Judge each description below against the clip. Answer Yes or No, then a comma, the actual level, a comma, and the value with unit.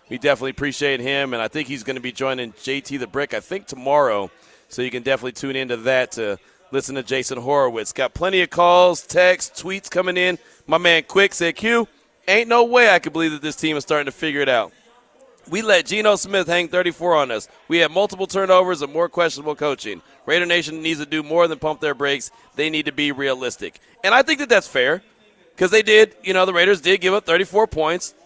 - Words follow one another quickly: Yes, fast, 225 wpm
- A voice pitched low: No, medium, 160 Hz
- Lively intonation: No, average, 4.8 semitones